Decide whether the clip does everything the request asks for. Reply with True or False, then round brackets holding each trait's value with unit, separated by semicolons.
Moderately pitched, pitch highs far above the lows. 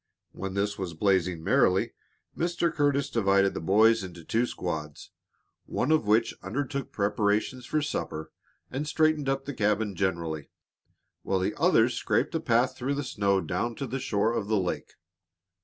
False (105 Hz; 5.9 semitones)